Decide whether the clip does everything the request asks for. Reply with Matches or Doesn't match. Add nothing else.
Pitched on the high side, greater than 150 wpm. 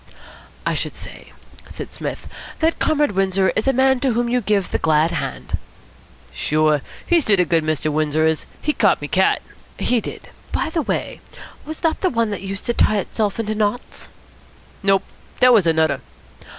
Matches